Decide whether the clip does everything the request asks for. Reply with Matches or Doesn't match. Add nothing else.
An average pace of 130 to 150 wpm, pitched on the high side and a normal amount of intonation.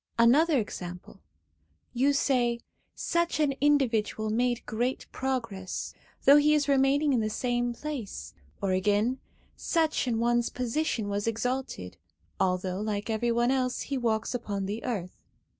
Matches